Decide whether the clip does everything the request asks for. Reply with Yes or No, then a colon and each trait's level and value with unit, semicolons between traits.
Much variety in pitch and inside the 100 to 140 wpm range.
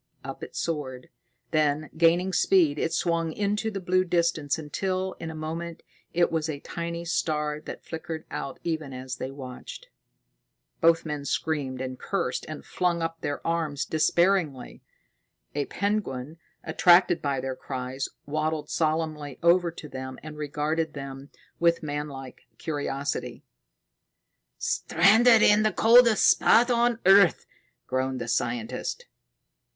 No: average, 3.3 semitones; slow, 135 wpm